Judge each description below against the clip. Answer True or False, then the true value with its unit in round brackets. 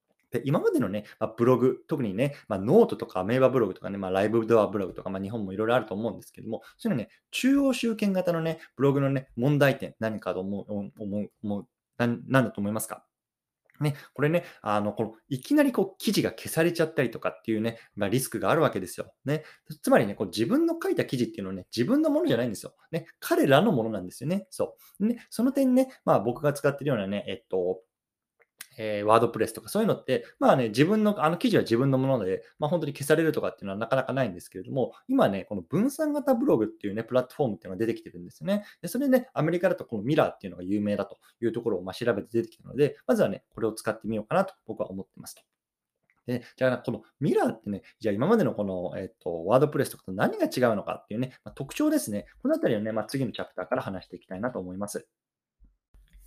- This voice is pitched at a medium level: False (125 Hz)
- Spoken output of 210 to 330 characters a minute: False (485 characters per minute)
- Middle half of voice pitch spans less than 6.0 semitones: False (7.8 semitones)